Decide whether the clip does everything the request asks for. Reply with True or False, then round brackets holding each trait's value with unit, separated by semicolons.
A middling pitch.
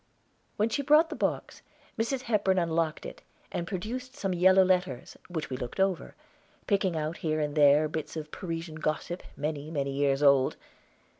True (165 Hz)